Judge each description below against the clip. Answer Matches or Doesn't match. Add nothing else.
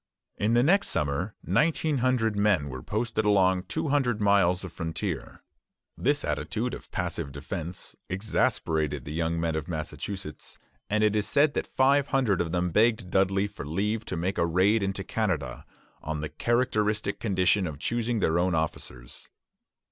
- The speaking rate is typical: Matches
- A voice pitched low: Matches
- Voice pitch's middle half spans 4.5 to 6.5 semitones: Matches